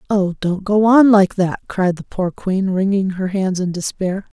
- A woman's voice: Yes, female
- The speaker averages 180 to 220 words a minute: Yes, fast, 205 wpm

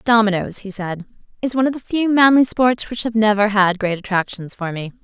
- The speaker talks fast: Yes, fast, 215 wpm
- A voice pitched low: No, high, 215 Hz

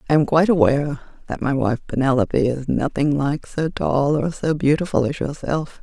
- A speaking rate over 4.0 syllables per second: Yes, 5.3 syllables/s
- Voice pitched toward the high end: No, medium, 145 Hz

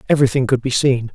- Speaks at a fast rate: Yes, fast, 210 wpm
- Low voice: Yes, low, 130 Hz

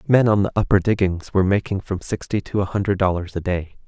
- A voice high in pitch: No, very low, 95 Hz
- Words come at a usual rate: No, fast, 230 wpm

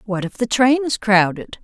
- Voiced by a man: No, female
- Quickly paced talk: Yes, fast, 220 wpm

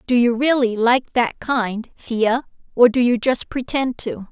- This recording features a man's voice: No, female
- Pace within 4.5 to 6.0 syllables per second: No, 3.9 syllables/s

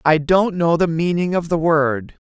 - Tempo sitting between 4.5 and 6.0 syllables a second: No, 4.3 syllables/s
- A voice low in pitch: No, medium, 170 Hz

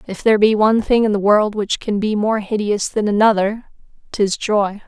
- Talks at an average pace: No, fast, 210 wpm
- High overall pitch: Yes, high, 210 Hz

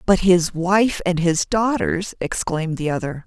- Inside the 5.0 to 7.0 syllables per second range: No, 4.3 syllables/s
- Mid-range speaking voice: Yes, medium, 180 Hz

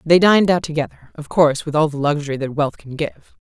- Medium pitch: Yes, medium, 155 Hz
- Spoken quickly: Yes, fast, 225 wpm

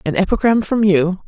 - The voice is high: Yes, high, 195 Hz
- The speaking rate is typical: Yes, average, 190 wpm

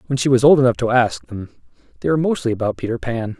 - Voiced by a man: Yes, male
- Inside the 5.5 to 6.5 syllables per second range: No, 6.9 syllables/s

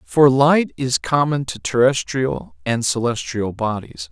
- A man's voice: Yes, male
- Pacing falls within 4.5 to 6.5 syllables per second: No, 3.9 syllables/s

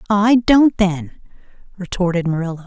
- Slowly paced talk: Yes, slow, 115 wpm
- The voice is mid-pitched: No, high, 195 Hz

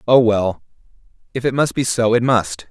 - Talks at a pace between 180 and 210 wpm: Yes, average, 200 wpm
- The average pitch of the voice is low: Yes, low, 115 Hz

